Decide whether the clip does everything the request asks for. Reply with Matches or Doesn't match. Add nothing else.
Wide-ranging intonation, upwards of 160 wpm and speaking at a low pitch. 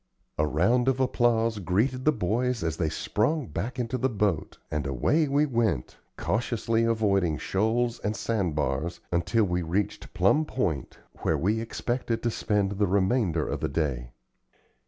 Doesn't match